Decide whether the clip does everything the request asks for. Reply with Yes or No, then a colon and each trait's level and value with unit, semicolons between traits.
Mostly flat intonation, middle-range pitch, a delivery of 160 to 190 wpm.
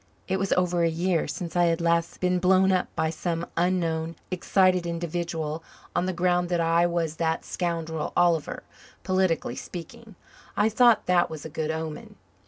Yes: narrow, 1.9 semitones; medium, 170 Hz; average, 170 wpm